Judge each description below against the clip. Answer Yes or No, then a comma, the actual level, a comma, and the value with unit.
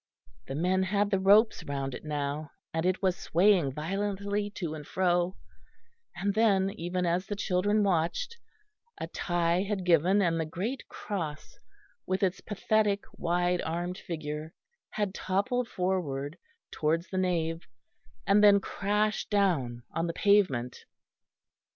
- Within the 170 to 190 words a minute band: No, average, 140 wpm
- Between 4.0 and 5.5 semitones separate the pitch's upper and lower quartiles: No, average, 3.5 semitones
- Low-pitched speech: No, medium, 180 Hz